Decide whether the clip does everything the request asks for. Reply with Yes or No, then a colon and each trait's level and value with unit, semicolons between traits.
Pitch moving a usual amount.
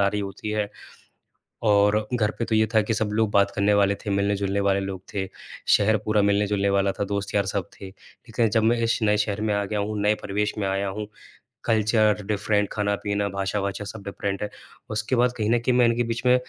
No: narrow, 1.4 semitones